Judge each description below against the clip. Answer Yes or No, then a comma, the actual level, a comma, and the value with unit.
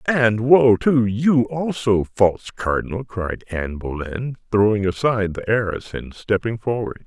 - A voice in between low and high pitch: No, low, 110 Hz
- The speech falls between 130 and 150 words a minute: Yes, average, 145 wpm